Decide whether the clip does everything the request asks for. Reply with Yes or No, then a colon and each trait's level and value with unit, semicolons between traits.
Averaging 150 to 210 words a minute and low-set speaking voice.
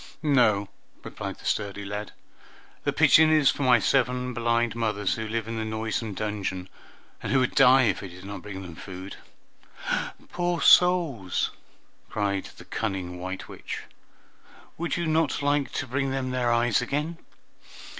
Yes: average, 155 wpm; low, 115 Hz